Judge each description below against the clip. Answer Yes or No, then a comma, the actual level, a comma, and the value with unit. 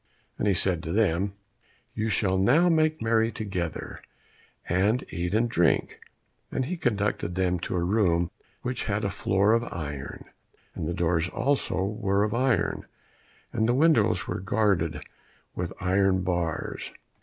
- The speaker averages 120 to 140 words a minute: No, average, 150 wpm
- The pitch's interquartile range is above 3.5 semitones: Yes, average, 4.4 semitones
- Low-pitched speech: Yes, low, 100 Hz